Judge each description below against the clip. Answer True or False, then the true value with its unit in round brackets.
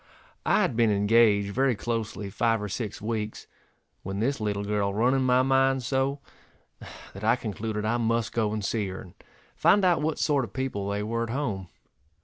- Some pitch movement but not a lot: True (3.8 semitones)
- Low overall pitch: True (115 Hz)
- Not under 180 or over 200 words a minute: True (190 wpm)